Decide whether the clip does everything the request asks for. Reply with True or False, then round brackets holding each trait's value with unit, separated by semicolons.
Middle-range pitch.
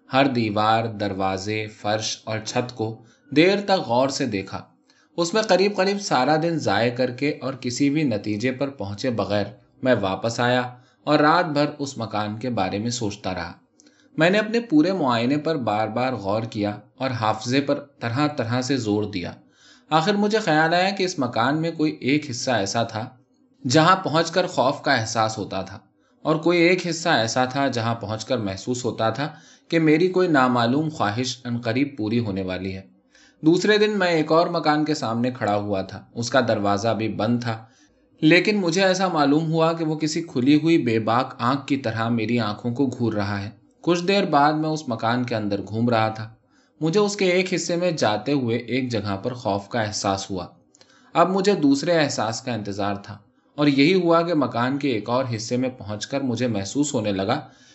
False (125 Hz)